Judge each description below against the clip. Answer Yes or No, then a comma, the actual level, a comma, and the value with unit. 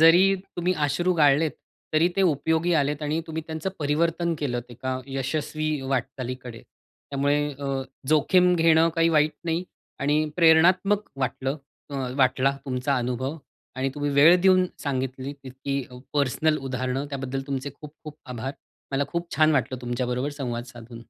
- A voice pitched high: No, medium, 145 Hz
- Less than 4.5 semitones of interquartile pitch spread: Yes, average, 3.7 semitones